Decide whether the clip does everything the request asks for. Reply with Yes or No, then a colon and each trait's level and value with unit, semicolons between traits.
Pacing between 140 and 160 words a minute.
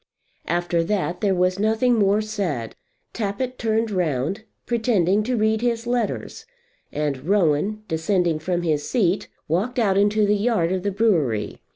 Yes: average, 150 wpm